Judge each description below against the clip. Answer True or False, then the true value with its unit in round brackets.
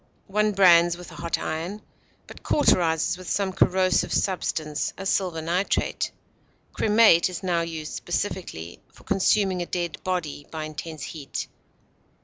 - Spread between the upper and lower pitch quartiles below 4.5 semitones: True (2.8 semitones)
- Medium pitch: True (175 Hz)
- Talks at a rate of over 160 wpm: False (135 wpm)